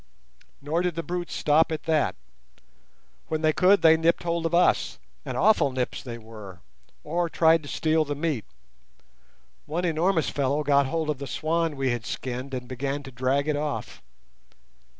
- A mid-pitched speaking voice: Yes, medium, 150 Hz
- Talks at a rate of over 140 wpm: Yes, average, 165 wpm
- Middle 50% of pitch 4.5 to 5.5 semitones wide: No, average, 3.5 semitones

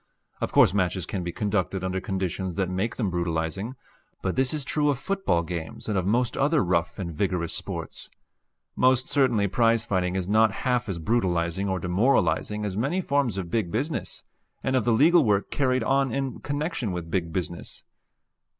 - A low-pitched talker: Yes, low, 100 Hz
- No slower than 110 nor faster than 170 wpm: No, average, 180 wpm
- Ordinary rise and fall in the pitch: No, wide, 6.0 semitones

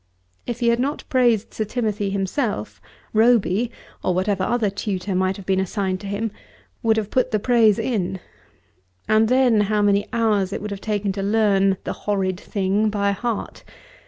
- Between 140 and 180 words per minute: Yes, average, 175 wpm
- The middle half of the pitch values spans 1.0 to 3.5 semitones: Yes, narrow, 2.5 semitones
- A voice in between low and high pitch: No, high, 210 Hz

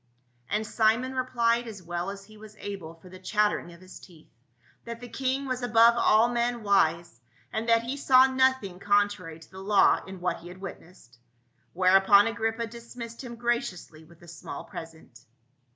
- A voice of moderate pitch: No, high, 210 Hz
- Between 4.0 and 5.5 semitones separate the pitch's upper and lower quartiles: Yes, average, 4.5 semitones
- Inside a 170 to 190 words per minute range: Yes, average, 180 wpm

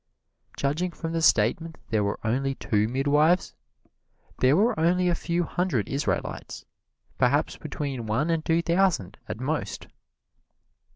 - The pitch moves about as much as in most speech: Yes, average, 4.9 semitones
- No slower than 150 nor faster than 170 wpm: No, slow, 135 wpm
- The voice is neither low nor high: Yes, medium, 150 Hz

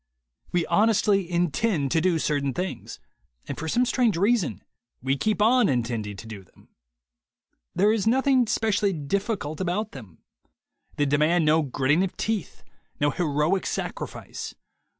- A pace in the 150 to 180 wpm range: No, average, 140 wpm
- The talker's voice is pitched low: No, medium, 175 Hz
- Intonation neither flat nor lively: No, wide, 6.5 semitones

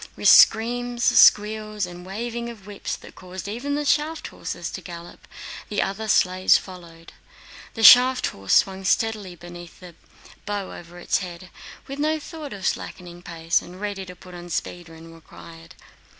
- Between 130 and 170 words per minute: Yes, average, 160 wpm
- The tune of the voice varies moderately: Yes, average, 4.3 semitones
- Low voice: No, high, 190 Hz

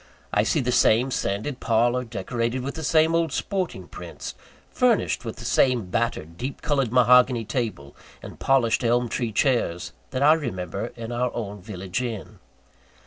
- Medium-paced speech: Yes, average, 160 wpm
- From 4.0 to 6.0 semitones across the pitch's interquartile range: No, average, 3.4 semitones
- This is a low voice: Yes, low, 120 Hz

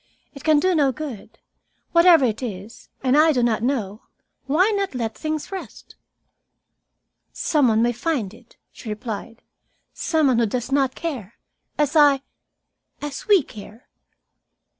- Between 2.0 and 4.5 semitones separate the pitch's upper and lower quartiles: No, average, 5.2 semitones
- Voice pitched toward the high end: Yes, very high, 265 Hz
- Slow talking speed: No, average, 145 wpm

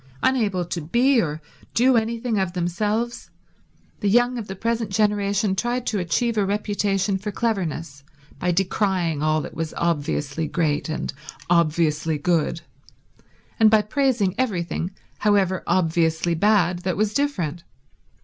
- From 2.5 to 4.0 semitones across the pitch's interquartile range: No, average, 4.5 semitones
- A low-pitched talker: No, high, 190 Hz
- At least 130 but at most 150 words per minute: Yes, slow, 135 wpm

